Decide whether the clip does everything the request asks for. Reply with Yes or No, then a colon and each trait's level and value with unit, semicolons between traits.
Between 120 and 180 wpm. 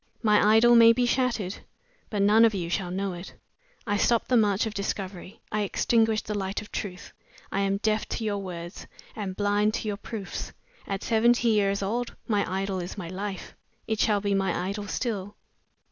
No: average, 190 wpm